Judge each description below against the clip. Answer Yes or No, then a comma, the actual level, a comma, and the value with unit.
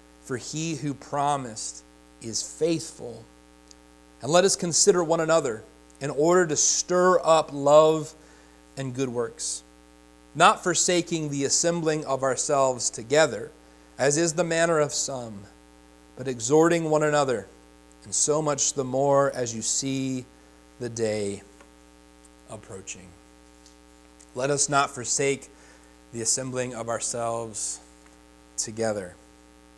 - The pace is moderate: No, slow, 115 wpm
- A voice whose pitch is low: Yes, low, 120 Hz